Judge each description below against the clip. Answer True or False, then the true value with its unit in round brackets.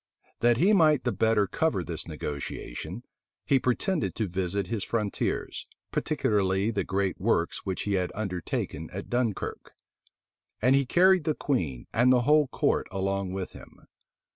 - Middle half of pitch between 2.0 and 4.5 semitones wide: False (5.3 semitones)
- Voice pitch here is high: False (105 Hz)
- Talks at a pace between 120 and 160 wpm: True (150 wpm)